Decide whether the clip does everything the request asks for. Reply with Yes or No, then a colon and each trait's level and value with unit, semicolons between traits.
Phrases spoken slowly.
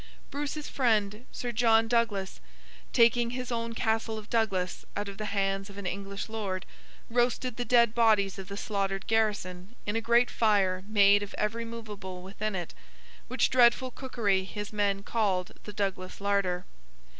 No: average, 160 wpm